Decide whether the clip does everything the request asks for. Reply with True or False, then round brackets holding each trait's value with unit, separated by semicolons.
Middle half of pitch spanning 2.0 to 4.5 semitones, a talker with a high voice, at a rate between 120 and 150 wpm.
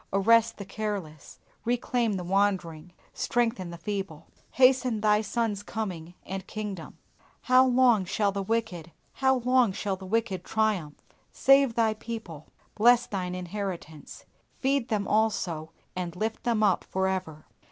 True (4.0 semitones; 205 Hz; 140 wpm)